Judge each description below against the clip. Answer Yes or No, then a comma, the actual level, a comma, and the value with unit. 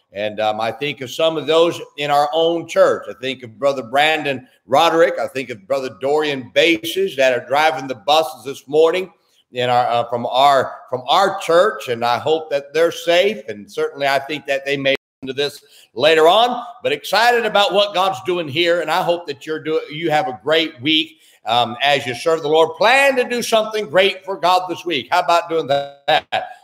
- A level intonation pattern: No, average, 4.1 semitones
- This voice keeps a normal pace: No, fast, 210 wpm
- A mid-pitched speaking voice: Yes, medium, 155 Hz